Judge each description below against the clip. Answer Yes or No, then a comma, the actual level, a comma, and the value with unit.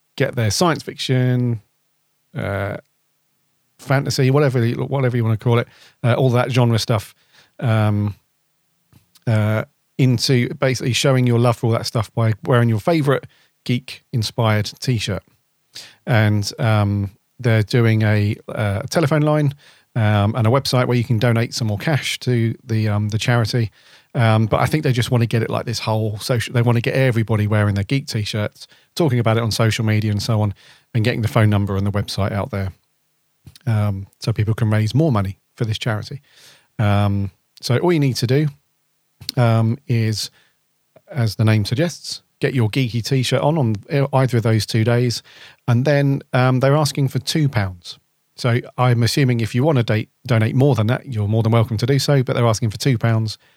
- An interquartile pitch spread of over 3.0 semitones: Yes, average, 3.5 semitones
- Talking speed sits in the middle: Yes, average, 190 wpm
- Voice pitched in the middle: No, low, 120 Hz